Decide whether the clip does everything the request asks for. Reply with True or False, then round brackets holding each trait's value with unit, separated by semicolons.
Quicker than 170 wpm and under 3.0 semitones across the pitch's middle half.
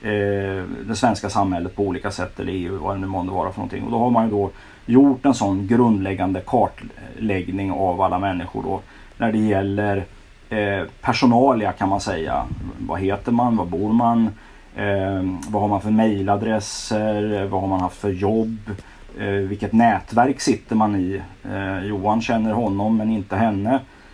False (160 wpm; 2.4 semitones)